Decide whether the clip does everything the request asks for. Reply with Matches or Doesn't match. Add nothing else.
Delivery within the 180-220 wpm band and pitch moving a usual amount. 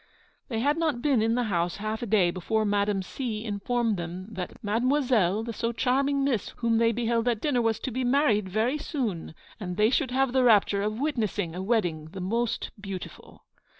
Matches